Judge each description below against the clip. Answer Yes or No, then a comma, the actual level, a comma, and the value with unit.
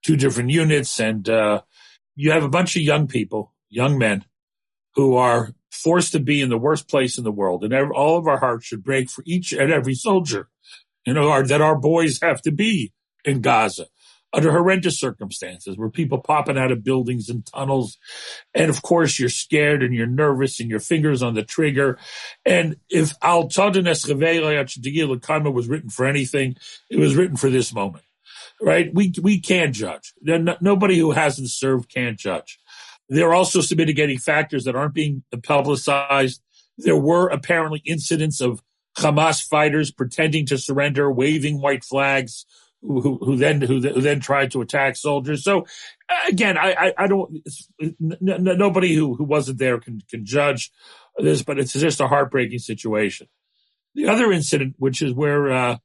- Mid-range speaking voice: Yes, medium, 145 Hz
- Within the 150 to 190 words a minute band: Yes, average, 175 wpm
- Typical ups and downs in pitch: Yes, average, 3.9 semitones